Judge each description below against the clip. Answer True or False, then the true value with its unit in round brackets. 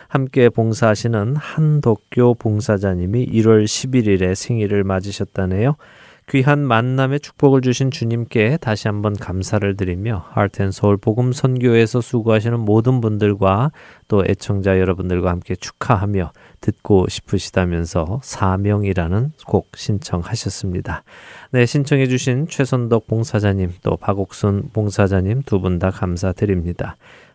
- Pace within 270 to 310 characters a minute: True (300 characters per minute)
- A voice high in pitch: False (105 Hz)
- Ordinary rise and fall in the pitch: True (4.3 semitones)